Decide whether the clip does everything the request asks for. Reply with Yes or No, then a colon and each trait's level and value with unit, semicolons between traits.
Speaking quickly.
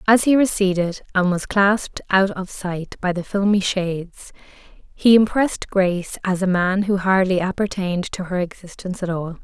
No: average, 170 wpm